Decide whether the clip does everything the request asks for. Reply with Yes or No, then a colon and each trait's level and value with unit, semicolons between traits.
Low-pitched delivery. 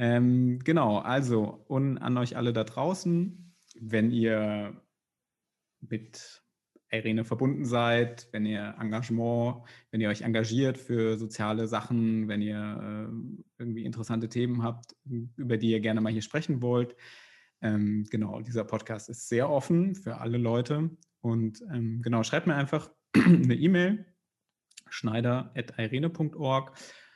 Yes: low, 120 Hz